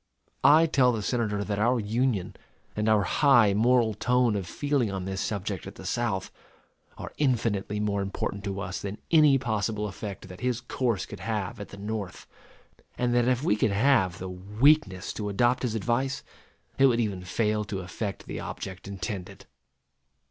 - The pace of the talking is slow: No, average, 175 wpm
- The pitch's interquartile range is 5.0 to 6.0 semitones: No, average, 3.8 semitones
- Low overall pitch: Yes, low, 105 Hz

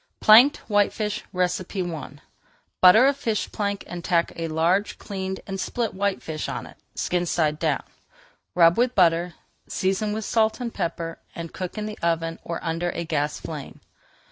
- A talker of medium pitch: Yes, medium, 180 Hz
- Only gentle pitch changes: No, average, 3.9 semitones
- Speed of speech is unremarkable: Yes, average, 160 wpm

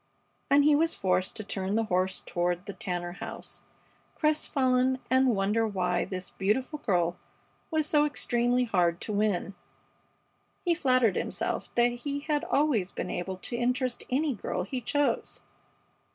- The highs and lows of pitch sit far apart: Yes, wide, 6.5 semitones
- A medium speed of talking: Yes, average, 150 wpm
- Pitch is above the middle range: Yes, high, 230 Hz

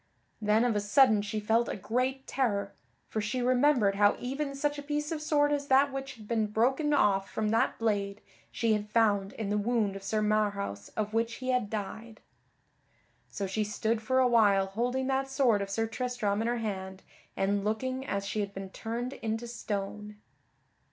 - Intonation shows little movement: No, average, 3.8 semitones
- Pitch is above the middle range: Yes, high, 220 Hz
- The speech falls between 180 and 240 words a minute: Yes, average, 190 wpm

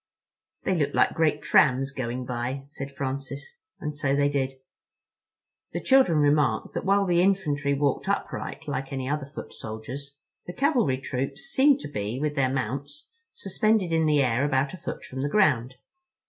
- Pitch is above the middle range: No, medium, 140 Hz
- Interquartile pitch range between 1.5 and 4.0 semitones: Yes, average, 3.5 semitones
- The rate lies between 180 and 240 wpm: No, average, 170 wpm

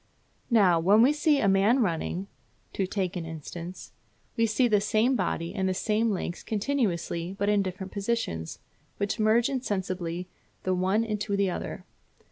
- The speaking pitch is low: No, high, 200 Hz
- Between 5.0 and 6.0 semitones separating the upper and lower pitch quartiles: No, average, 3.4 semitones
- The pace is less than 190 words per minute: Yes, average, 160 wpm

